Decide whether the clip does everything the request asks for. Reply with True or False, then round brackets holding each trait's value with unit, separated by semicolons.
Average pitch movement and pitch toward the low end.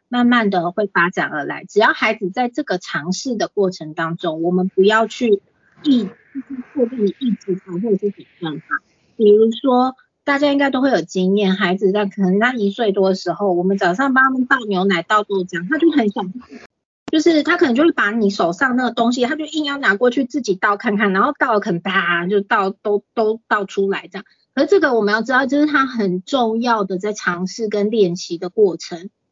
False (4.9 semitones; 210 Hz)